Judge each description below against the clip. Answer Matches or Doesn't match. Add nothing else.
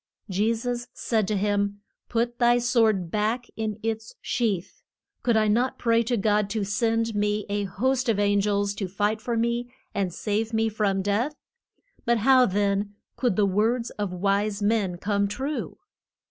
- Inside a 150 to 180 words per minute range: Matches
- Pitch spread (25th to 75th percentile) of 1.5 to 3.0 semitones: Matches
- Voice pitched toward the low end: Doesn't match